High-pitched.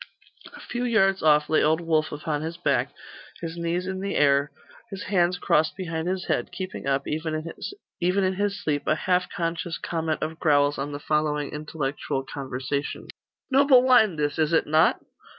No: medium, 160 Hz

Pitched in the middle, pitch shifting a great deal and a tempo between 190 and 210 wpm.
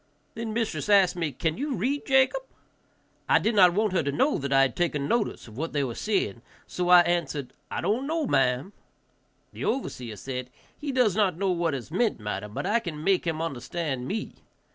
Yes: medium, 175 Hz; wide, 7.7 semitones; fast, 205 wpm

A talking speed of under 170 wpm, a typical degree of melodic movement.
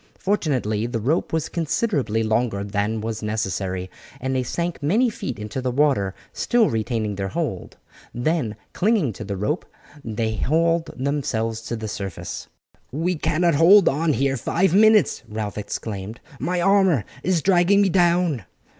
No: average, 150 wpm; wide, 7.9 semitones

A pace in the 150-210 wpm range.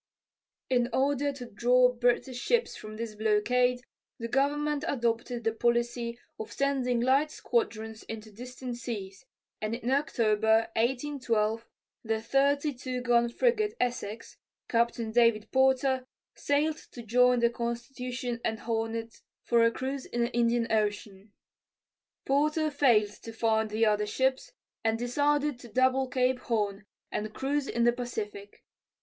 No: slow, 135 wpm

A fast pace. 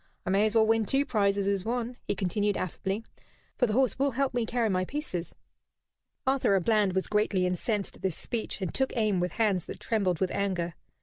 Yes: fast, 210 wpm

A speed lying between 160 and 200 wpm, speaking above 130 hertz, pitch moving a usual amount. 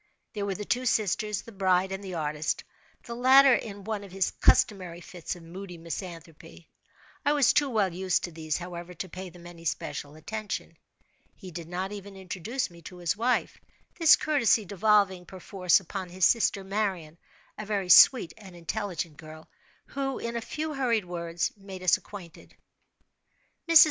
Yes: average, 165 wpm; high, 190 Hz; average, 3.7 semitones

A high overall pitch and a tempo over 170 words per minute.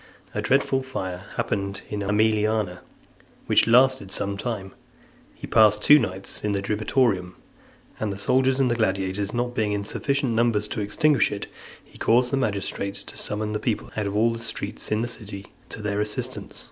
No: low, 105 Hz; average, 180 wpm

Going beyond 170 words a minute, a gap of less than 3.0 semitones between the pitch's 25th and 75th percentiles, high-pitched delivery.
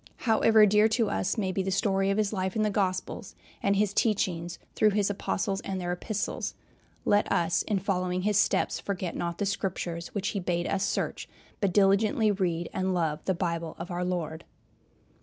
Yes: average, 190 wpm; narrow, 2.6 semitones; high, 195 Hz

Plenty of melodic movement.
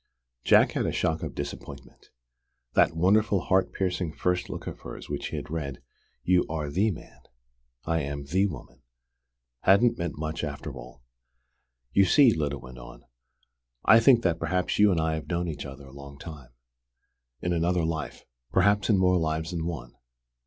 No: average, 4.3 semitones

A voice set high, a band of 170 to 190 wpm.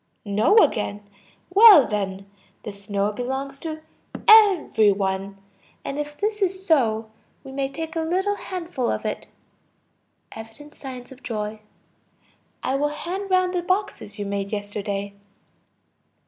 No: very high, 265 Hz; slow, 135 wpm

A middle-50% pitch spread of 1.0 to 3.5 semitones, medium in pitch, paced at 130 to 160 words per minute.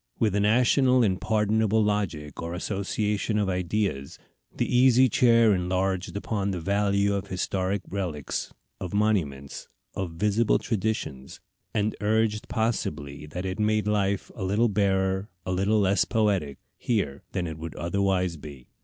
No: average, 2.9 semitones; low, 100 Hz; average, 145 wpm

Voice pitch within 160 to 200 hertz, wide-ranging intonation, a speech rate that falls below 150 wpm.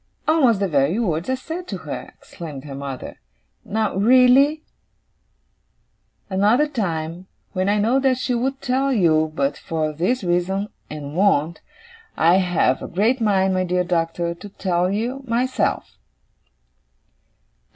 Yes: high, 190 Hz; wide, 6.8 semitones; average, 140 wpm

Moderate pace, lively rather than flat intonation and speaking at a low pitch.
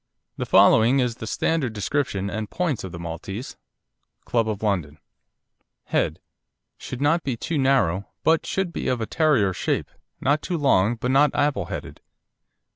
Yes: average, 160 wpm; wide, 6.4 semitones; low, 120 Hz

